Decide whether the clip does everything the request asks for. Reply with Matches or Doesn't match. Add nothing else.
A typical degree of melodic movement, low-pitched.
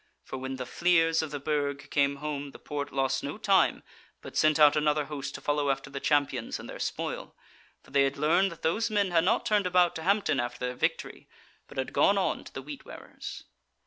Doesn't match